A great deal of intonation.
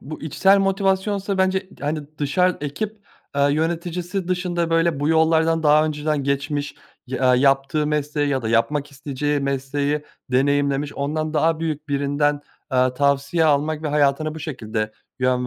No: narrow, 2.6 semitones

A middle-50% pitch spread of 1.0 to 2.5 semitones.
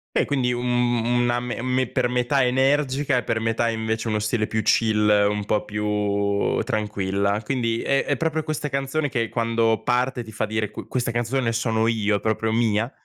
No: average, 2.9 semitones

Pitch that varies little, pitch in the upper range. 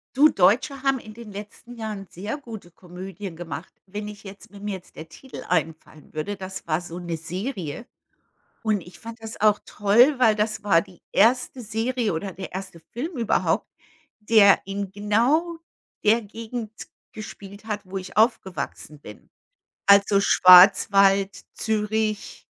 No: average, 3.0 semitones; high, 205 Hz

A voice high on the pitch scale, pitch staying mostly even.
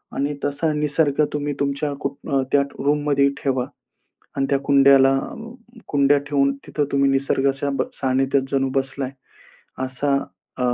No: medium, 140 Hz; narrow, 1.1 semitones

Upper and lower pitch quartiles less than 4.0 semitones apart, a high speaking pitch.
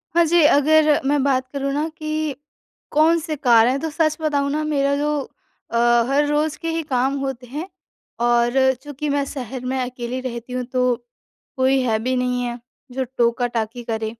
Yes: average, 3.4 semitones; very high, 270 Hz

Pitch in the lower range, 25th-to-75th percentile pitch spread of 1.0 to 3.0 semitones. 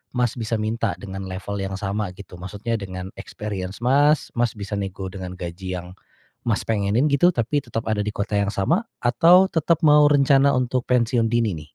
No: low, 110 Hz; average, 4.6 semitones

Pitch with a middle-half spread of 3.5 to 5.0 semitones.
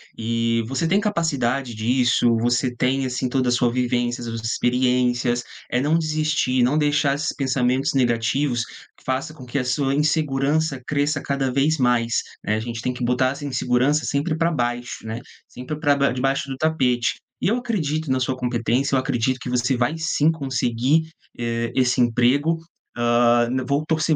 No: average, 3.0 semitones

